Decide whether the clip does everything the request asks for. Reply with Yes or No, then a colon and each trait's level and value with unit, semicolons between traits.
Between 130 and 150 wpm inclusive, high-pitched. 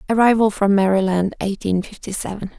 Yes: average, 140 wpm; high, 200 Hz